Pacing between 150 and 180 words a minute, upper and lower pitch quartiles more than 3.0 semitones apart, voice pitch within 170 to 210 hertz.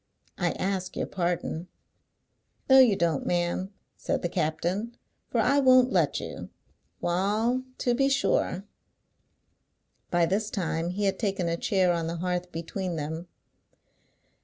No: slow, 135 wpm; average, 4.0 semitones; medium, 185 Hz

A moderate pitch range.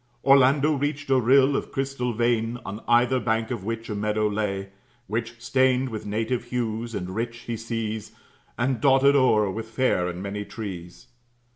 Yes: average, 3.3 semitones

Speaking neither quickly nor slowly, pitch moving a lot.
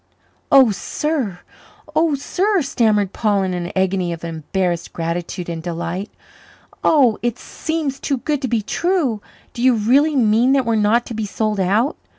Yes: average, 160 wpm; wide, 6.4 semitones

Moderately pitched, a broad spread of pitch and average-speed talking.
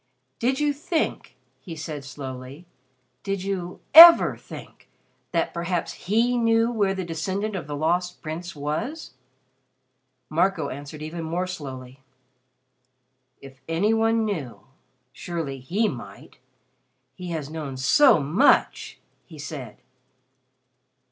No: medium, 170 Hz; wide, 6.4 semitones; slow, 120 wpm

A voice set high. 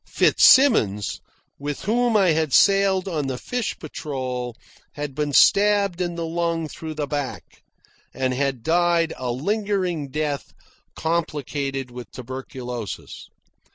No: medium, 150 Hz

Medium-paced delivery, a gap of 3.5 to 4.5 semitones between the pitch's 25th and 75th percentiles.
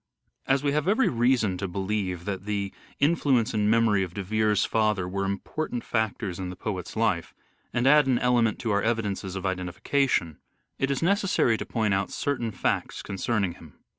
Yes: average, 190 wpm; average, 4.2 semitones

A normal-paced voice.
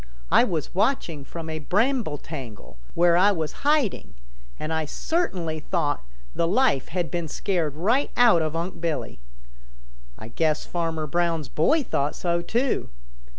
Yes: average, 150 wpm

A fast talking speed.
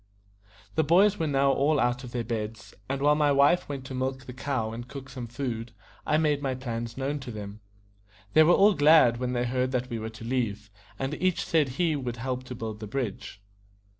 Yes: fast, 220 wpm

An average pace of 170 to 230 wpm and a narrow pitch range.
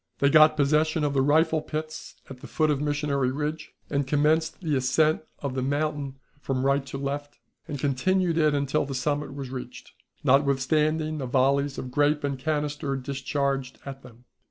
Yes: average, 175 wpm; narrow, 2.1 semitones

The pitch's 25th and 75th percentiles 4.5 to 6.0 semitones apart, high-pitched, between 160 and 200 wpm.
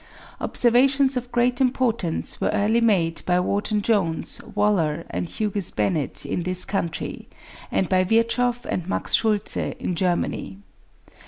No: average, 4.9 semitones; high, 205 Hz; slow, 135 wpm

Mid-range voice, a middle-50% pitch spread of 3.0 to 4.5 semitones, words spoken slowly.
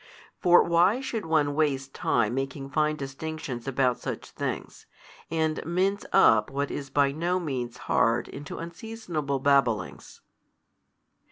Yes: medium, 145 Hz; average, 3.7 semitones; slow, 125 wpm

